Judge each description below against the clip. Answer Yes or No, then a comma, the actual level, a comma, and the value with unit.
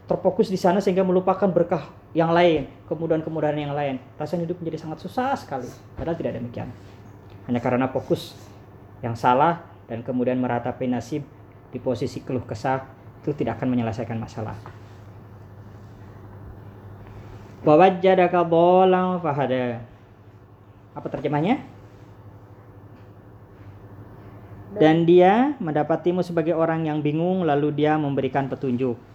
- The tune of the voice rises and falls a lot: Yes, wide, 7.9 semitones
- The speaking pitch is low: Yes, low, 130 Hz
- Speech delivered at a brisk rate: No, average, 115 wpm